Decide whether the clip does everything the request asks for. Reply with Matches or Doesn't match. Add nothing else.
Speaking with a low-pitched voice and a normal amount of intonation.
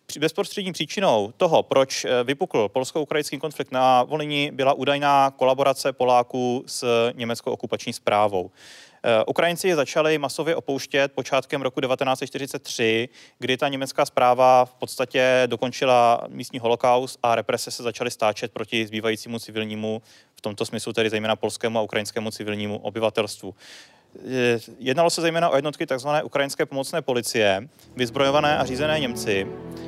Matches